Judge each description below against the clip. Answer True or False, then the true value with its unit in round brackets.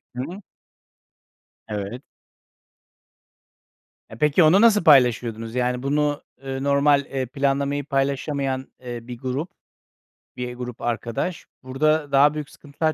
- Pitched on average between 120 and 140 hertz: True (135 Hz)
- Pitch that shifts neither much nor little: True (3.0 semitones)